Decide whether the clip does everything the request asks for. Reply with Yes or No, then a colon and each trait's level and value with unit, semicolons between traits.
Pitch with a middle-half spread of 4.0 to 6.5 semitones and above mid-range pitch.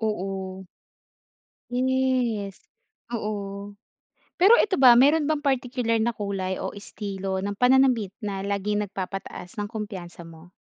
Yes: average, 4.3 semitones; high, 205 Hz